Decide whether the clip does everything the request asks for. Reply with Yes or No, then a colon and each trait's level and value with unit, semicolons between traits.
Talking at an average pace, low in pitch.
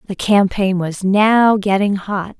No: average, 150 wpm; high, 200 Hz